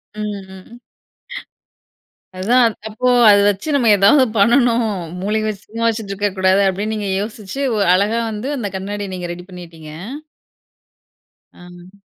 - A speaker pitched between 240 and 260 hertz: No, high, 205 Hz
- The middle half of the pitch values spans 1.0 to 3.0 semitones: Yes, average, 2.7 semitones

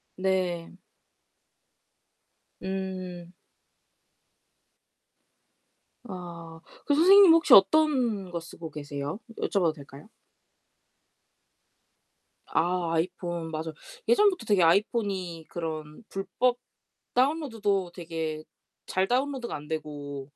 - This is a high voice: No, medium, 180 Hz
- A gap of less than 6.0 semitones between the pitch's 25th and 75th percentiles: Yes, wide, 5.4 semitones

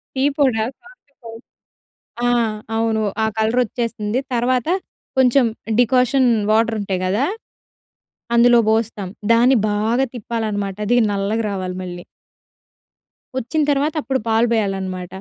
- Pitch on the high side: Yes, high, 230 Hz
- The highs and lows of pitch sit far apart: No, average, 3.4 semitones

